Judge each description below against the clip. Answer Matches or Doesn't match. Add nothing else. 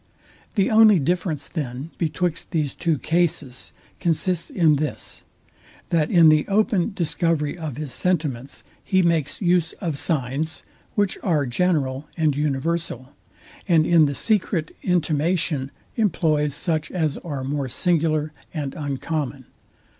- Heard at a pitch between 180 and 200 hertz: Doesn't match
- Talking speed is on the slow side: Matches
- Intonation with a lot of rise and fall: Doesn't match